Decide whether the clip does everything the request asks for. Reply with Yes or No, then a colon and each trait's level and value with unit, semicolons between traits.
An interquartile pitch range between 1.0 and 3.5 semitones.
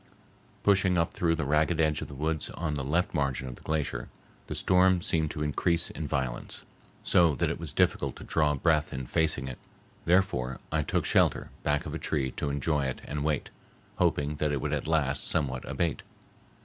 Yes: average, 2.8 semitones